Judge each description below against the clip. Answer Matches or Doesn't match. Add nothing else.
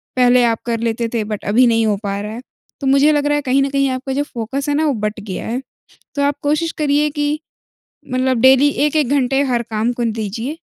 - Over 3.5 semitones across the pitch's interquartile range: Matches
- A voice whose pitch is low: Doesn't match